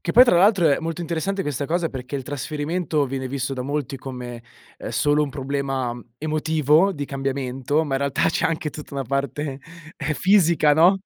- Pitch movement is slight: No, average, 3.1 semitones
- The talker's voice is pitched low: No, medium, 145 Hz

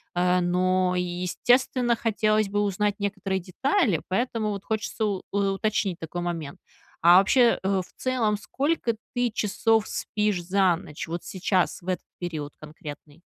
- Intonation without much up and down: No, average, 3.4 semitones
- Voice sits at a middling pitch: No, high, 195 Hz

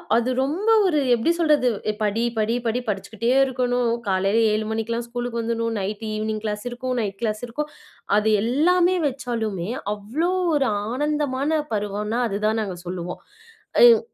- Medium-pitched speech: No, high, 230 Hz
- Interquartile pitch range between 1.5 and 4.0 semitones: Yes, average, 3.7 semitones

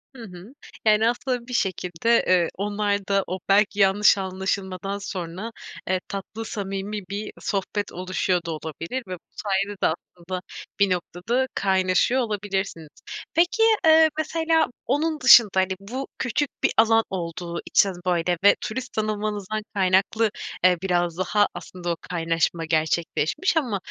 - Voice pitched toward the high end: Yes, high, 195 Hz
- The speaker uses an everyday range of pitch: Yes, average, 3.5 semitones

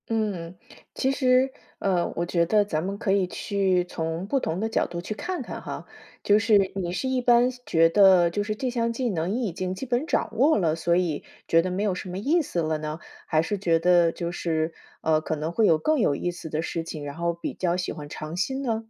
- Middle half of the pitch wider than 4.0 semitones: Yes, average, 4.9 semitones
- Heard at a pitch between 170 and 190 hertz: Yes, medium, 185 Hz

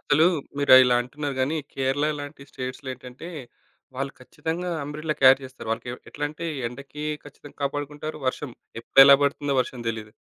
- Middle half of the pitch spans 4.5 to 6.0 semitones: No, narrow, 2.4 semitones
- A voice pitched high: No, medium, 140 Hz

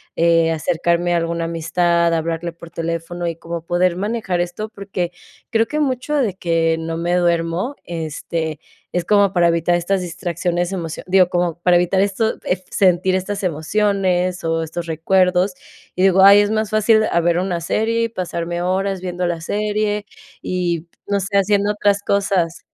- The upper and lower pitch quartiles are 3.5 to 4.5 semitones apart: No, average, 2.9 semitones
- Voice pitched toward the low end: No, medium, 180 Hz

